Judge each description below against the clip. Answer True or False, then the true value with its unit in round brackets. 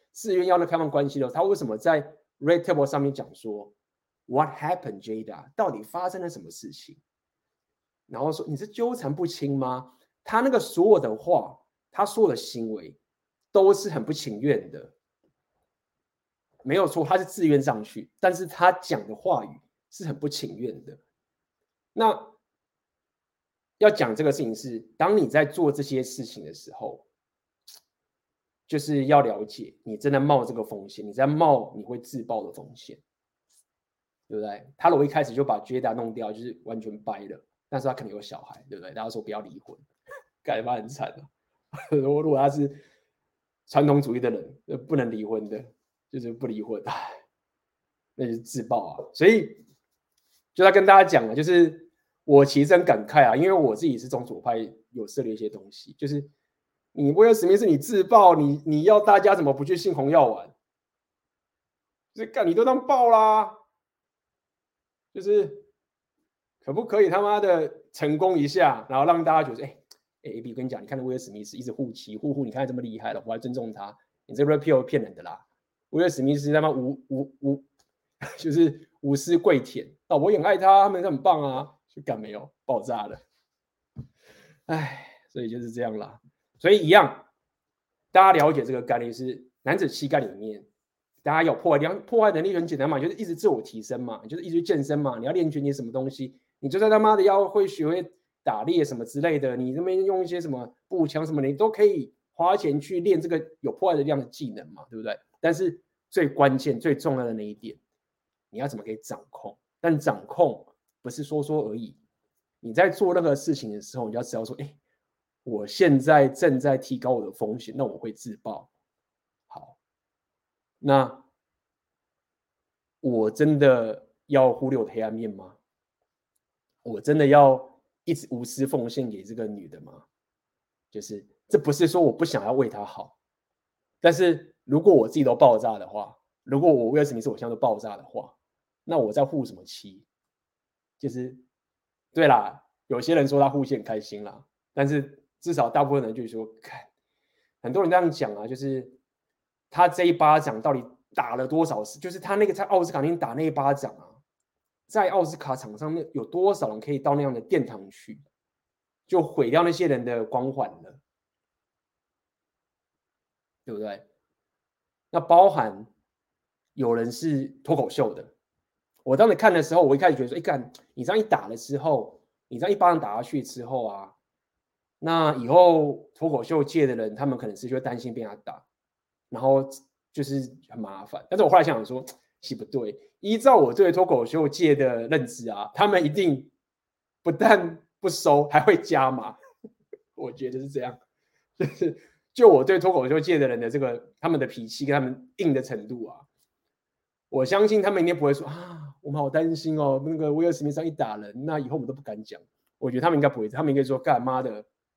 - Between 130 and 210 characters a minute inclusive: False (275 characters per minute)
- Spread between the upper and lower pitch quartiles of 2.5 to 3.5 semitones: False (5.1 semitones)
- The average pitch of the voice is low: False (145 Hz)